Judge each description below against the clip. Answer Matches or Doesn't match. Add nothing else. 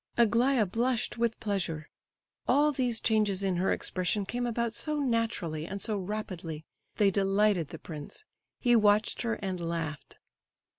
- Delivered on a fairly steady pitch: Doesn't match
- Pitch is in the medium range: Doesn't match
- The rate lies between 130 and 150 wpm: Matches